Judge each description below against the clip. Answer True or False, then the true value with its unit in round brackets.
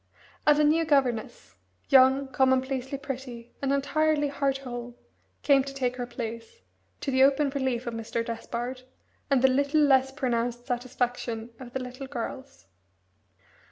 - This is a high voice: True (260 Hz)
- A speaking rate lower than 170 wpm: True (145 wpm)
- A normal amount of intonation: False (2.3 semitones)